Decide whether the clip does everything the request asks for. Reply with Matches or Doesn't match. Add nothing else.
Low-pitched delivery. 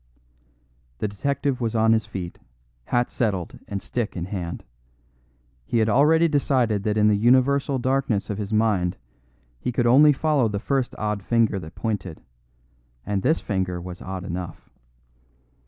Matches